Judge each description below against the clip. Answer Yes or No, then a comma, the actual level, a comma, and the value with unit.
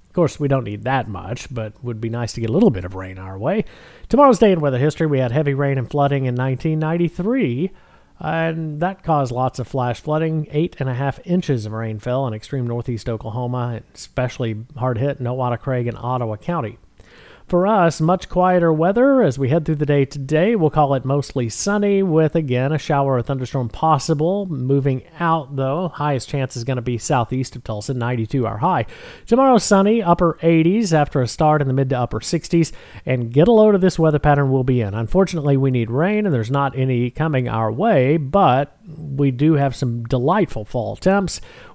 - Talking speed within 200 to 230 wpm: Yes, fast, 205 wpm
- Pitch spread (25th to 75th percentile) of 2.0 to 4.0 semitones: No, average, 4.7 semitones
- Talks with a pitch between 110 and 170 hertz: Yes, medium, 140 Hz